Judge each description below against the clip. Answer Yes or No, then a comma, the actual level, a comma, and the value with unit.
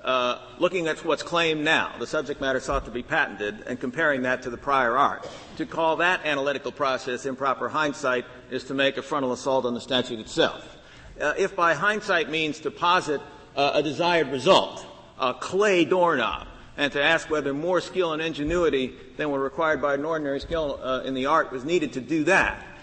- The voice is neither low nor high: Yes, medium, 145 Hz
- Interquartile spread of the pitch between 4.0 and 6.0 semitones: Yes, average, 4.4 semitones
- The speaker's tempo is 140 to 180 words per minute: No, average, 195 wpm